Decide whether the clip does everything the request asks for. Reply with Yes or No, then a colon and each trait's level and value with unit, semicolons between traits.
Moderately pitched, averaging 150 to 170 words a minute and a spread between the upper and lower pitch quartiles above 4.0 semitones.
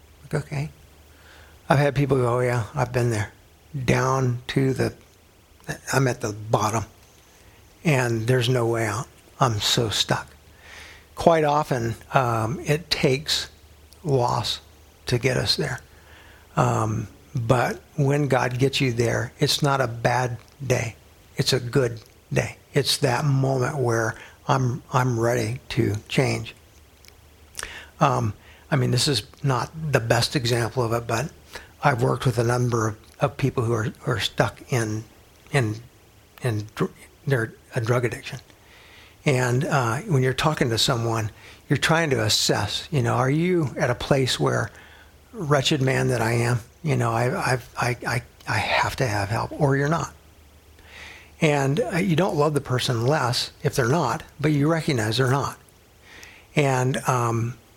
No: low, 120 Hz; average, 160 wpm; average, 4.4 semitones